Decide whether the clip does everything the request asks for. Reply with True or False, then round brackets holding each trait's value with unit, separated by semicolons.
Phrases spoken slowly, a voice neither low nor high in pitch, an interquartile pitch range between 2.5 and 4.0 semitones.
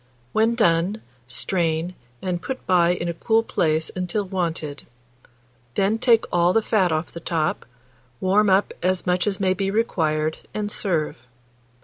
False (150 wpm; 180 Hz; 3.7 semitones)